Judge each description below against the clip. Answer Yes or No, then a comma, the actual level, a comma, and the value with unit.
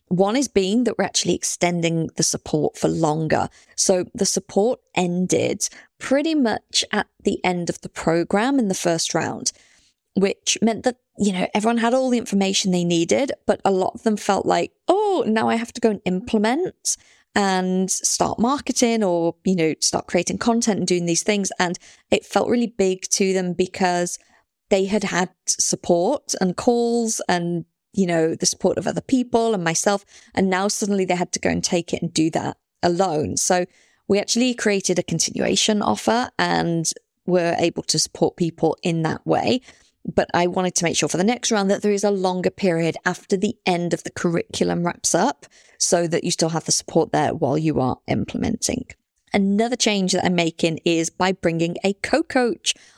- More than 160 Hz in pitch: Yes, high, 190 Hz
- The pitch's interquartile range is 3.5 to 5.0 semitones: Yes, average, 3.9 semitones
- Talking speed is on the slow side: No, average, 190 wpm